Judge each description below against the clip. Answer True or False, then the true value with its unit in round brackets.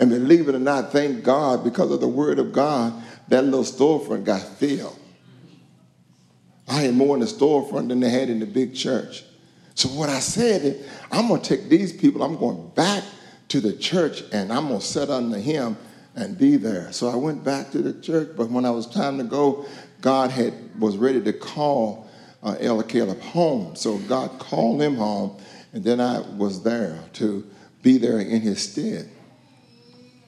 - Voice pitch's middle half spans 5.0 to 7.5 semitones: False (3.1 semitones)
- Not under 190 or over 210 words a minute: True (195 wpm)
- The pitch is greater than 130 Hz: False (125 Hz)